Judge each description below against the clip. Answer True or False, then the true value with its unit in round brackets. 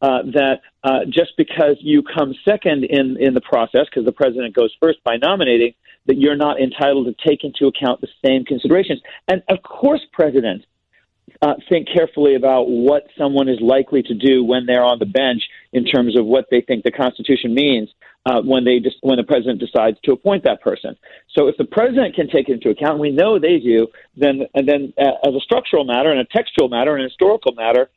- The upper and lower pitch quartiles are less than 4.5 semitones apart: True (3.1 semitones)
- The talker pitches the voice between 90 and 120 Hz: False (135 Hz)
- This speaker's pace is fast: True (215 wpm)